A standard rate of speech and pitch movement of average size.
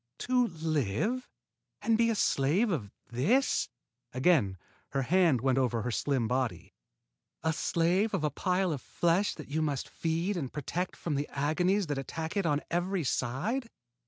No: average, 160 wpm; wide, 5.7 semitones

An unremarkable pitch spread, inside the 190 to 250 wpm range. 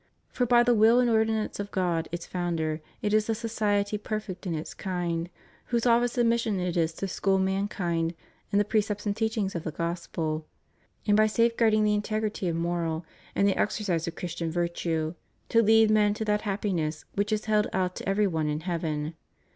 Yes: average, 4.1 semitones; average, 195 wpm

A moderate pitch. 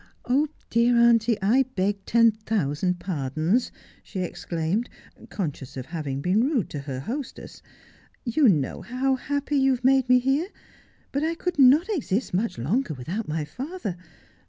No: high, 225 Hz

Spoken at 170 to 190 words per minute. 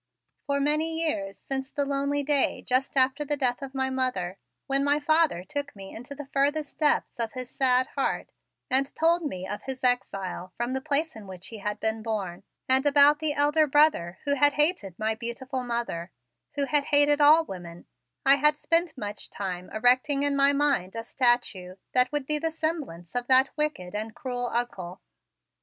Yes: average, 185 wpm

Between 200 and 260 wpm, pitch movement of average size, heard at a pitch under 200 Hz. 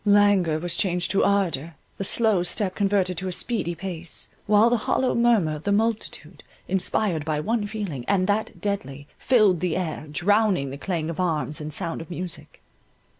No: average, 175 wpm; average, 4.0 semitones; medium, 185 Hz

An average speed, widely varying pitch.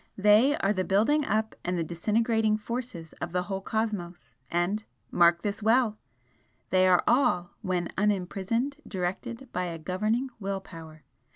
No: average, 150 wpm; average, 3.9 semitones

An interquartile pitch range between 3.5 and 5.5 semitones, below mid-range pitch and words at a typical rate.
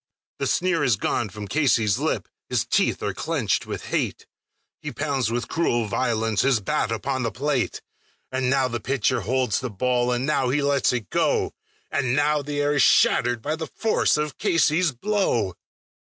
Yes: average, 3.9 semitones; low, 130 Hz; average, 180 wpm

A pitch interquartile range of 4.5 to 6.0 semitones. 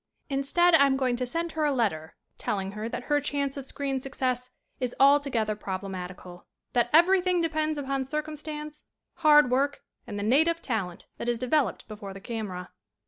Yes: wide, 5.6 semitones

